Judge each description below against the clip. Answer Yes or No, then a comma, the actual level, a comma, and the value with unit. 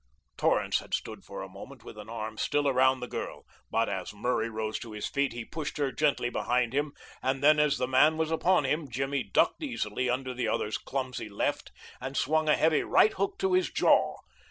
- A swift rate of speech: Yes, fast, 210 wpm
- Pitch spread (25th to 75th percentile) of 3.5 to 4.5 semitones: Yes, average, 3.9 semitones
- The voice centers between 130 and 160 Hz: Yes, low, 135 Hz